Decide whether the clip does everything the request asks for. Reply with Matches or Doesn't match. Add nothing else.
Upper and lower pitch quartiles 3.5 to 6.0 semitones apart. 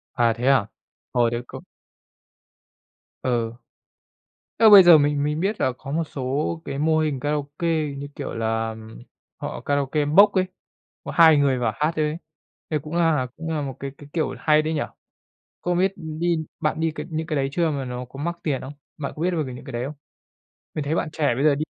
Doesn't match